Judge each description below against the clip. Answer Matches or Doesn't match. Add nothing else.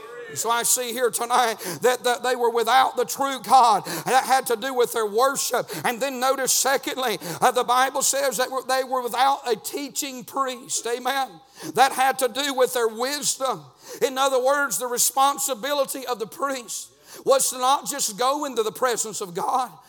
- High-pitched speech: Matches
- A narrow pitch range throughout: Matches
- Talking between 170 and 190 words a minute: Matches